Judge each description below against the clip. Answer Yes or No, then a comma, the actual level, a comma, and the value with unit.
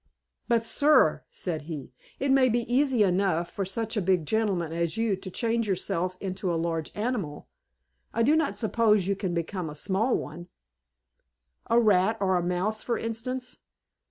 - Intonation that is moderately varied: Yes, average, 4.5 semitones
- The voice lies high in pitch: Yes, high, 200 Hz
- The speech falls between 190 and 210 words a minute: No, average, 165 wpm